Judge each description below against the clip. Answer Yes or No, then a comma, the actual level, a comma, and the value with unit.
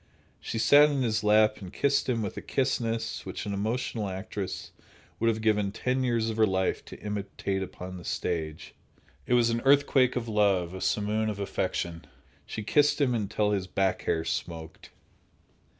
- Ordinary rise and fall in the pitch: Yes, average, 3.4 semitones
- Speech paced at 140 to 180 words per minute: Yes, average, 175 wpm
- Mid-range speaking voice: No, low, 110 Hz